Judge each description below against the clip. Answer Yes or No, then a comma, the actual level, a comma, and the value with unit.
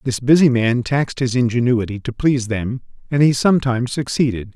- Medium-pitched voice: No, low, 125 Hz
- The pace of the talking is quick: No, average, 170 wpm